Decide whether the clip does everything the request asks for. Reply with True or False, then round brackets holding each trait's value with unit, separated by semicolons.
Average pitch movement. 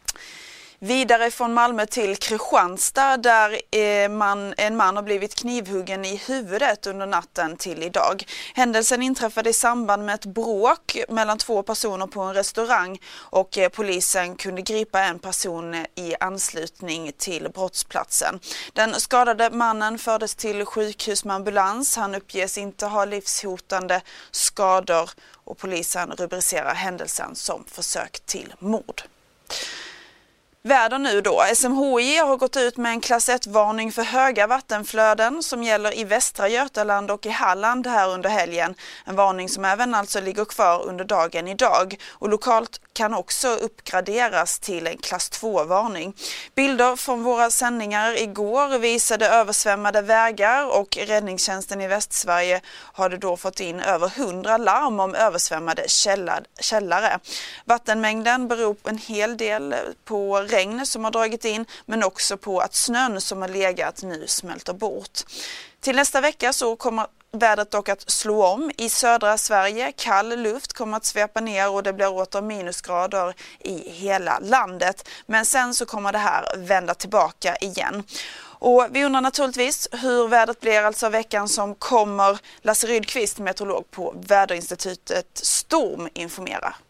True (3.4 semitones)